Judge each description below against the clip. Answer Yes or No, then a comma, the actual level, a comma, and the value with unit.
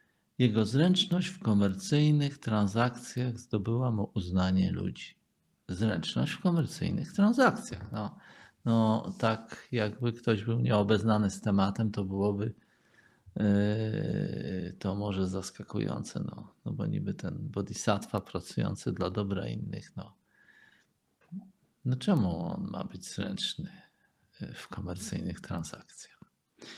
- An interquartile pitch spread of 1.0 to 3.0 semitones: No, average, 4.3 semitones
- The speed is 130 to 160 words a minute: No, slow, 110 wpm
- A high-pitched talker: No, low, 110 Hz